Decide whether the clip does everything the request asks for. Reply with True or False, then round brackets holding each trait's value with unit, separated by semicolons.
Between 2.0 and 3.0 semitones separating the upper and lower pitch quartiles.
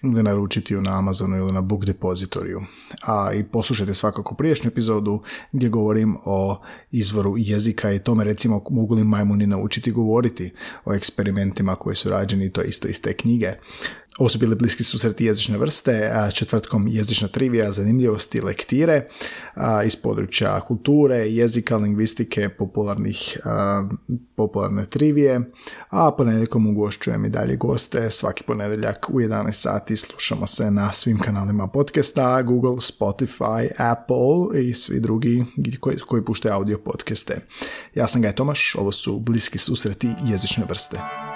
True (2.7 semitones)